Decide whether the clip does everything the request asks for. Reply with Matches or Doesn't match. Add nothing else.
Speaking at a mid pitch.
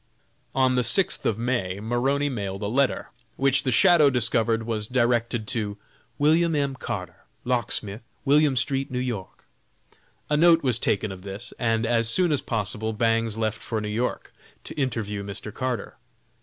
Doesn't match